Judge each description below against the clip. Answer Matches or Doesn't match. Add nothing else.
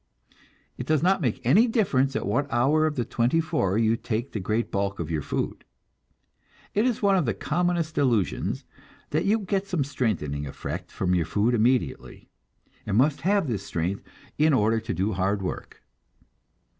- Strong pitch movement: Matches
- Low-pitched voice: Matches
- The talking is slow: Doesn't match